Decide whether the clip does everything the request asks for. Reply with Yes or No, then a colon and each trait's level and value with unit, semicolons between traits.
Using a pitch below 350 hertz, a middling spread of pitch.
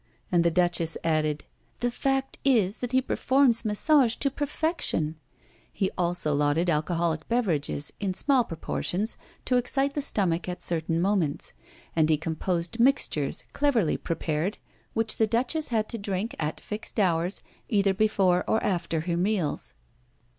No: high, 190 Hz; wide, 6.2 semitones